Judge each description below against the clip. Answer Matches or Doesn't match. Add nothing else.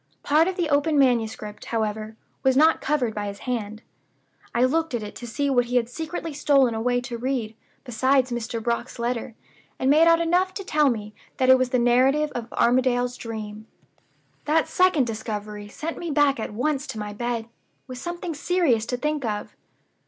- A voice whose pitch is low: Doesn't match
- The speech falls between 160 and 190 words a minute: Matches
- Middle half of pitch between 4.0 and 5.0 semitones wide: Matches